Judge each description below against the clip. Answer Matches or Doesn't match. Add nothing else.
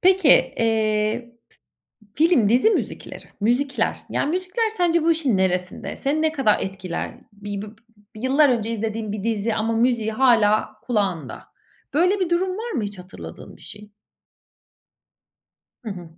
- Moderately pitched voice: Doesn't match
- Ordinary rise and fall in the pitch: Doesn't match